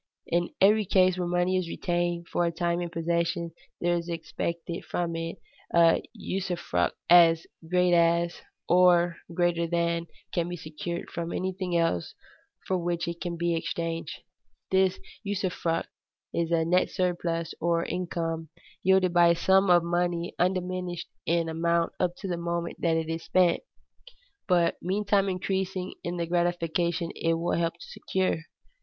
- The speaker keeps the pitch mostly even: Yes, narrow, 1.2 semitones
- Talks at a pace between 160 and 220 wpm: No, average, 150 wpm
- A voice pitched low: No, medium, 170 Hz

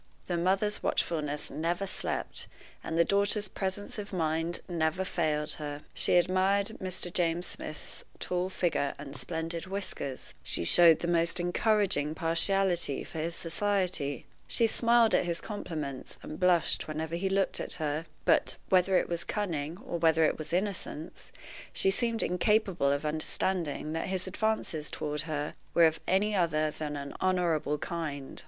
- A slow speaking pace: No, average, 155 wpm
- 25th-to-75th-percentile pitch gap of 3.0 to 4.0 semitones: Yes, average, 3.5 semitones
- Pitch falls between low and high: Yes, medium, 170 Hz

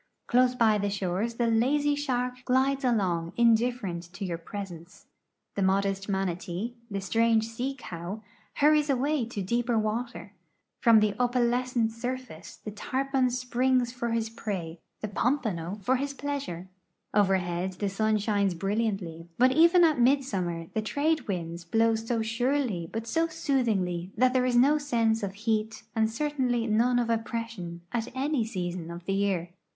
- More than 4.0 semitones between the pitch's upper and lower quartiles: Yes, average, 4.4 semitones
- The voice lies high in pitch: Yes, high, 225 Hz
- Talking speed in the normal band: Yes, average, 150 wpm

